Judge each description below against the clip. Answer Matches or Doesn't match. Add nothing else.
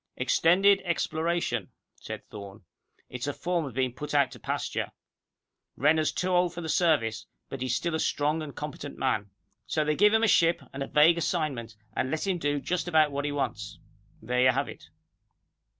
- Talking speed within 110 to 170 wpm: Doesn't match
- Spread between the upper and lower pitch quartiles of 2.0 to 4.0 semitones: Doesn't match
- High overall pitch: Doesn't match